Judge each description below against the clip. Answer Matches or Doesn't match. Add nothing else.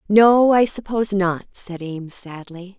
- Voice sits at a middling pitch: Doesn't match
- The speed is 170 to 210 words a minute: Doesn't match